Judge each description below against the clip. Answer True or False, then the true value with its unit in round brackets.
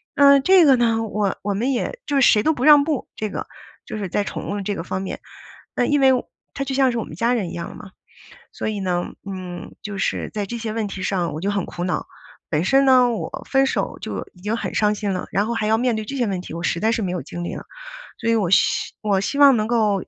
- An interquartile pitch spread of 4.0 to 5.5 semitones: True (4.5 semitones)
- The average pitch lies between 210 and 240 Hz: True (215 Hz)